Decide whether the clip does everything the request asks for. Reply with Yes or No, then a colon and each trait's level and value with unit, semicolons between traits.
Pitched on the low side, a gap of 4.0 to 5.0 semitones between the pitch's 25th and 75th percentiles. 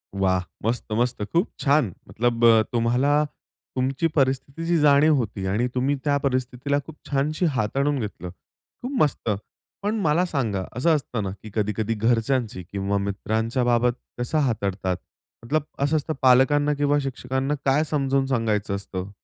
Yes: low, 130 Hz; average, 4.6 semitones